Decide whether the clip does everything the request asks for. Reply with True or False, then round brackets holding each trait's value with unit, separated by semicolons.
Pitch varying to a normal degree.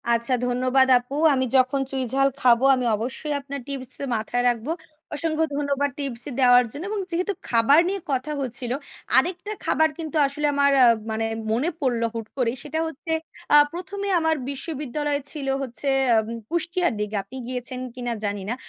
True (3.6 semitones)